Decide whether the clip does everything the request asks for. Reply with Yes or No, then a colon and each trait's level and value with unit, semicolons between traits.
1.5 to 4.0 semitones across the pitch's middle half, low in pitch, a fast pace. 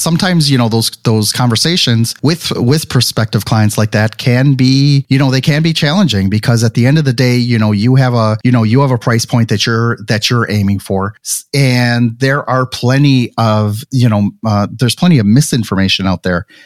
Yes: average, 3.6 semitones; low, 120 Hz; fast, 215 wpm